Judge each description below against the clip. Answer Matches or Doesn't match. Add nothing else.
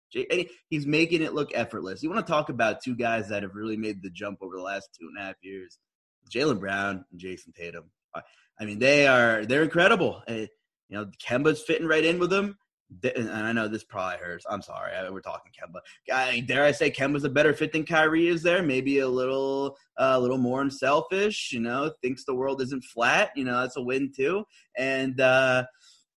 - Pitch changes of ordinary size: Doesn't match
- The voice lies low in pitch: Matches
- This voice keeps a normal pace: Doesn't match